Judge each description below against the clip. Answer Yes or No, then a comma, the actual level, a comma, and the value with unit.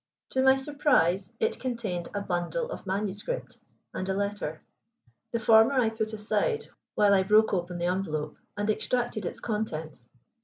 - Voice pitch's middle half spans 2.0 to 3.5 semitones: No, average, 4.4 semitones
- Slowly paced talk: No, average, 155 wpm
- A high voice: Yes, high, 205 Hz